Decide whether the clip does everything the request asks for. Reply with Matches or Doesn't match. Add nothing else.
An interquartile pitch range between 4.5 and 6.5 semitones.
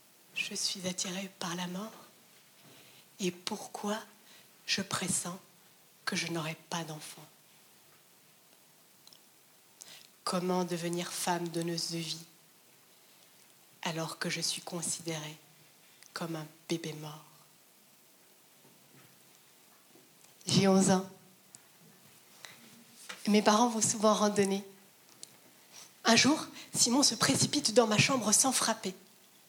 Doesn't match